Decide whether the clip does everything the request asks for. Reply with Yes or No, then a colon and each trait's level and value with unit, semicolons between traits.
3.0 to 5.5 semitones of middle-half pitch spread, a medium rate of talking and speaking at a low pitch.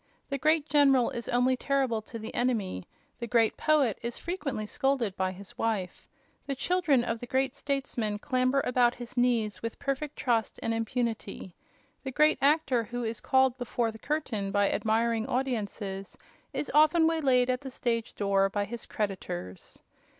No: average, 3.7 semitones; average, 165 wpm; high, 245 Hz